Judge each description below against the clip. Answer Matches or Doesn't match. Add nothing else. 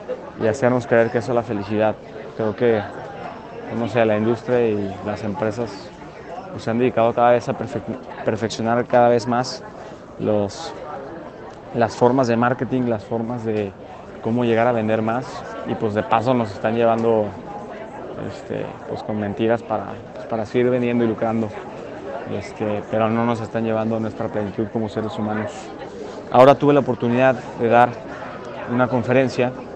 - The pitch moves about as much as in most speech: Doesn't match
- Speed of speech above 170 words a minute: Doesn't match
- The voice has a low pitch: Matches